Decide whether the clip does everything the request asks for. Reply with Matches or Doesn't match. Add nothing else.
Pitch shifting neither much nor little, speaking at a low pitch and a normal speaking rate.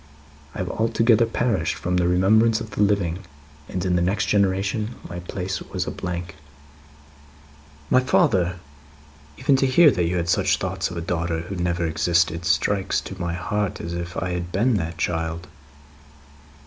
Matches